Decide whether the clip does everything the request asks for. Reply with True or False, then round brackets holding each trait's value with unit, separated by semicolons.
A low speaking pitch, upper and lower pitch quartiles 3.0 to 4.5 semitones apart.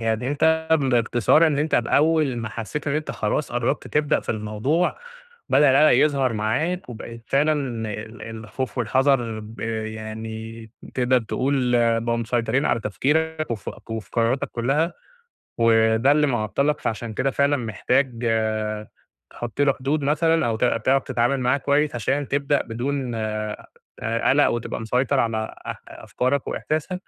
True (125 Hz; 4.1 semitones)